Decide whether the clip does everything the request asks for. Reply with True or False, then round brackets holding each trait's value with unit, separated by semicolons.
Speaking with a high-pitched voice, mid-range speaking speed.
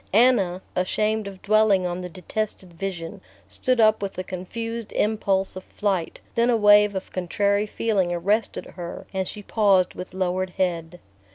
True (195 Hz; 160 wpm)